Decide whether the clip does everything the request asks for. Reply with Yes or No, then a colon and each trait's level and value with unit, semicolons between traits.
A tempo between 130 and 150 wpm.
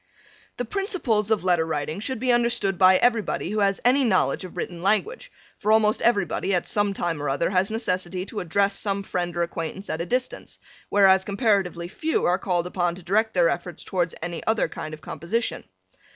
No: average, 195 wpm